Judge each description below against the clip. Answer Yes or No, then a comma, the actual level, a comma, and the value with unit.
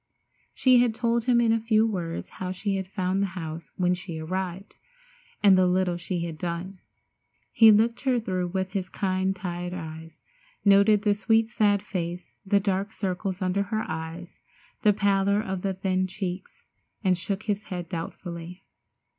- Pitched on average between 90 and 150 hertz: No, high, 190 Hz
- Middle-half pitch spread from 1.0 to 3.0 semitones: Yes, narrow, 2.4 semitones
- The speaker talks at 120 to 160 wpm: No, average, 170 wpm